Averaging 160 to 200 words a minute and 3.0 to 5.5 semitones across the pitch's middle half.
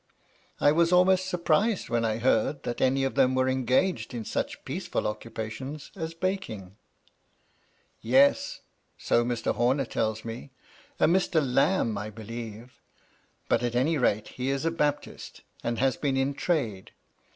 No: average, 150 wpm; average, 5.0 semitones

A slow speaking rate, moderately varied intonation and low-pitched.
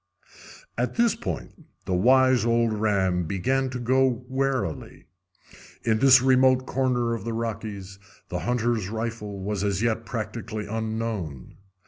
Yes: slow, 130 wpm; average, 3.6 semitones; low, 115 Hz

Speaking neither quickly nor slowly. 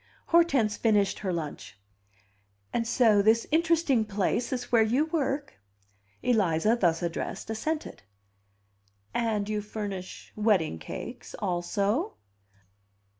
No: slow, 105 wpm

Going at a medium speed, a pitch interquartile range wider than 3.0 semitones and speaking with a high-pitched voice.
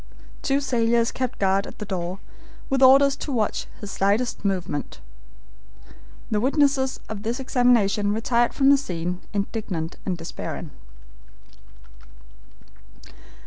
No: slow, 115 wpm; average, 5.1 semitones; high, 225 Hz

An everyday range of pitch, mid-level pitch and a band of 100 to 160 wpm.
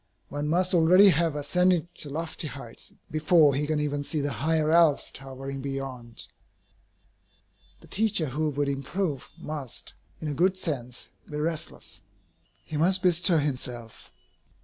Yes: average, 3.5 semitones; medium, 150 Hz; average, 140 wpm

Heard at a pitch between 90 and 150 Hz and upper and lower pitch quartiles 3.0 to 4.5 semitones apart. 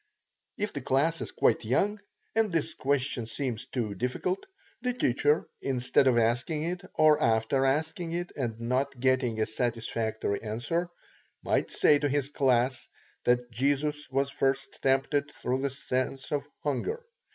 Yes: low, 135 Hz; average, 3.5 semitones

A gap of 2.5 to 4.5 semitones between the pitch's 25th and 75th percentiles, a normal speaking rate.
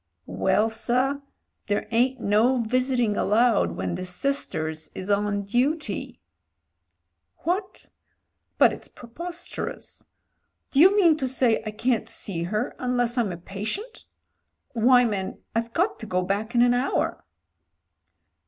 No: average, 4.2 semitones; slow, 130 wpm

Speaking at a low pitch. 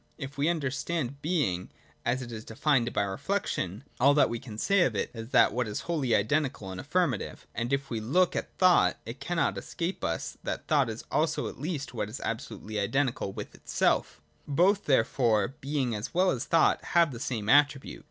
Yes: low, 130 Hz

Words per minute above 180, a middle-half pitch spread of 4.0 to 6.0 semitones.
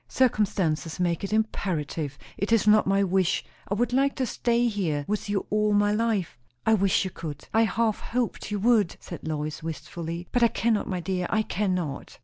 Yes: average, 190 wpm; average, 4.5 semitones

